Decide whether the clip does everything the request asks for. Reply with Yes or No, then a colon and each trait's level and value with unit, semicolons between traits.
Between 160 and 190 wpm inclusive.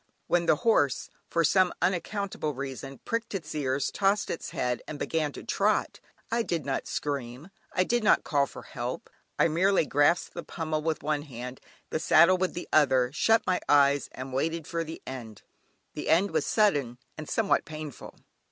Yes: average, 180 wpm